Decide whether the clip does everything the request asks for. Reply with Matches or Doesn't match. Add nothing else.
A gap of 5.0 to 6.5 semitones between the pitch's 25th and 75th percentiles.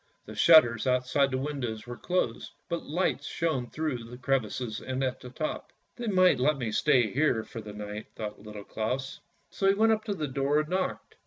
Matches